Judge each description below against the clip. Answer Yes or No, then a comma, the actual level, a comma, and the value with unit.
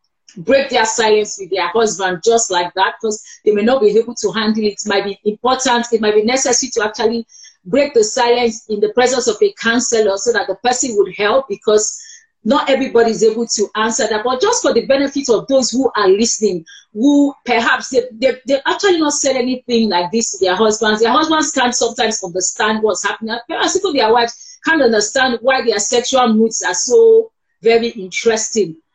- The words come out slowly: No, average, 200 wpm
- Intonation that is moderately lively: Yes, average, 3.7 semitones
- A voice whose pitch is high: Yes, high, 230 Hz